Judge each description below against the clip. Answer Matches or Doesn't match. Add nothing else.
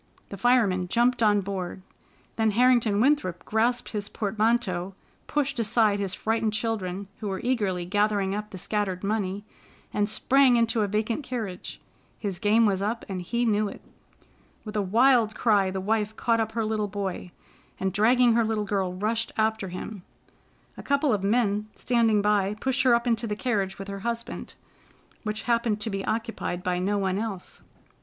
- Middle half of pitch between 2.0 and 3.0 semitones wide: Matches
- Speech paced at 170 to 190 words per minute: Matches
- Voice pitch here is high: Matches